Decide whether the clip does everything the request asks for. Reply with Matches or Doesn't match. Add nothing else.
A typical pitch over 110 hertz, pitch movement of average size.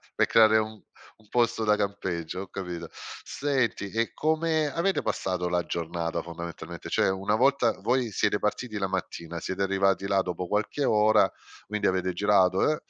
Doesn't match